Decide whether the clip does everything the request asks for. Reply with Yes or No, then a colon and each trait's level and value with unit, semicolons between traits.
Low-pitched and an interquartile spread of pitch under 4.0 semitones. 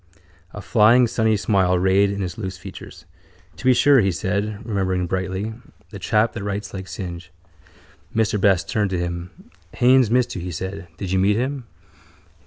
Yes: low, 100 Hz; average, 2.9 semitones